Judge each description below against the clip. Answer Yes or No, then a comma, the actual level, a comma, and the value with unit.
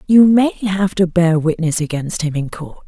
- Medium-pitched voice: Yes, medium, 175 Hz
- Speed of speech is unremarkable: No, fast, 210 wpm